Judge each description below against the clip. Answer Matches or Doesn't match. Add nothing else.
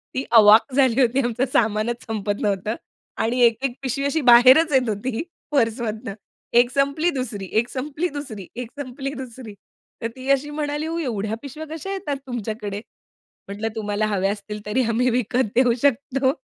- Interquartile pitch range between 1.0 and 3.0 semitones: Doesn't match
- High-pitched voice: Matches